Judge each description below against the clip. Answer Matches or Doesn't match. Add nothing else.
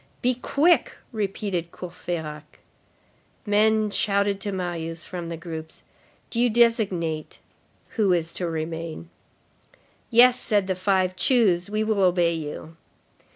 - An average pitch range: Matches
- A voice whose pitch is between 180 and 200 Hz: Matches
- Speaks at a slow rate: Matches